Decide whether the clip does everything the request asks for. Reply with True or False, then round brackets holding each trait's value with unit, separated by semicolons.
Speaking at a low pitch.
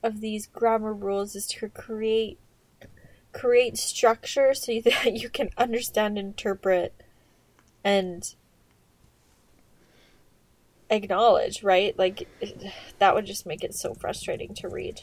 False (220 Hz)